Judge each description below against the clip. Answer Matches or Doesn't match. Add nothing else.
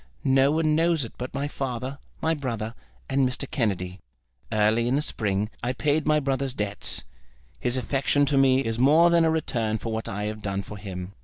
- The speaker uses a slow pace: Doesn't match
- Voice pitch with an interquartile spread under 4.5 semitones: Doesn't match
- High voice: Doesn't match